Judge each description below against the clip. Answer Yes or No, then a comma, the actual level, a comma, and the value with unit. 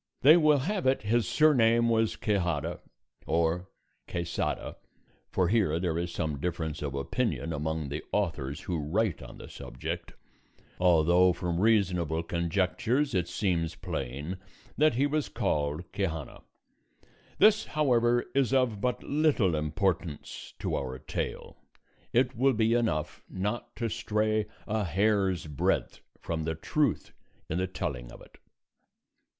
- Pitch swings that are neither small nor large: No, wide, 6.5 semitones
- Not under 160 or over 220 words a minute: No, slow, 135 wpm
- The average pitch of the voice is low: Yes, very low, 95 Hz